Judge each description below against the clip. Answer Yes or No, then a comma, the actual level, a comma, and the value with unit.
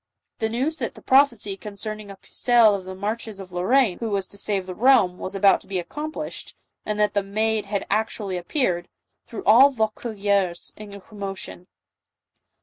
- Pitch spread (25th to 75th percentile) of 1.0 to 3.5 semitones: Yes, narrow, 2.6 semitones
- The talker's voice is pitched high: Yes, high, 210 Hz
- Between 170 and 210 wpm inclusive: Yes, average, 175 wpm